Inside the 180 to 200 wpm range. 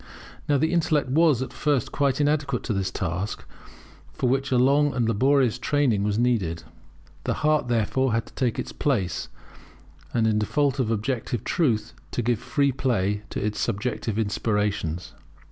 No: average, 160 wpm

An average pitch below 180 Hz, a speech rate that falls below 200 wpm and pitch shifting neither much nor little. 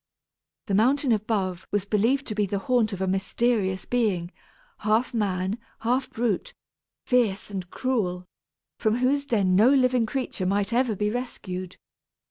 No: high, 215 Hz; average, 145 wpm; average, 4.3 semitones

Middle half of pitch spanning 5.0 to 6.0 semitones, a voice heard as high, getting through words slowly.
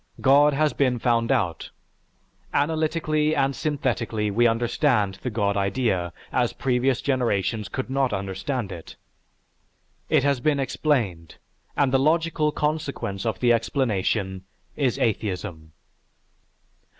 No: wide, 5.6 semitones; low, 125 Hz; slow, 115 wpm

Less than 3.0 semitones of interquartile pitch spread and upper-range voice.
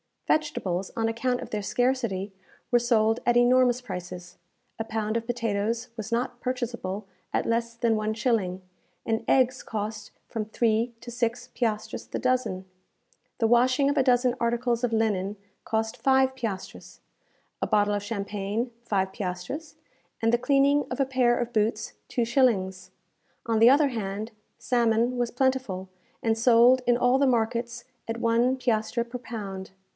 Yes: narrow, 2.5 semitones; high, 235 Hz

